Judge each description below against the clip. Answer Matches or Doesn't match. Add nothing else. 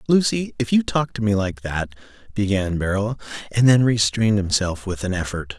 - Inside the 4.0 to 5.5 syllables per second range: Matches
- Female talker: Doesn't match